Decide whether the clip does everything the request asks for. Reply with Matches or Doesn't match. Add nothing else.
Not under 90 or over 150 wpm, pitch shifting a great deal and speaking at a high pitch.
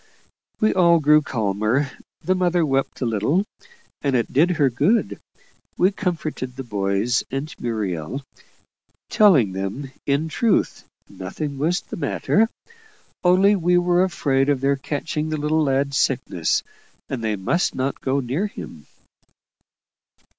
Doesn't match